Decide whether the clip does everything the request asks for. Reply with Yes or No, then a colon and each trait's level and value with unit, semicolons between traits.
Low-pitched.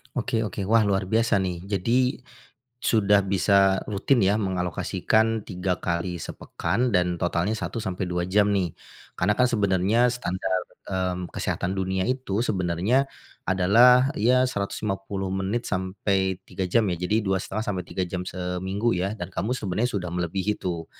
Yes: very low, 95 Hz